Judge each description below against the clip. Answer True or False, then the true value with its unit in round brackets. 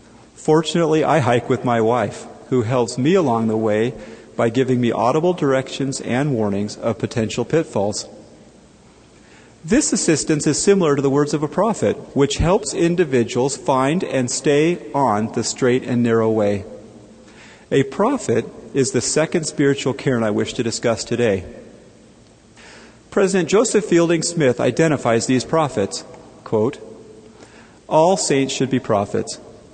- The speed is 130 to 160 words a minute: True (140 wpm)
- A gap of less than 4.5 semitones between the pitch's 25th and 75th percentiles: False (5.2 semitones)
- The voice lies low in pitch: True (130 Hz)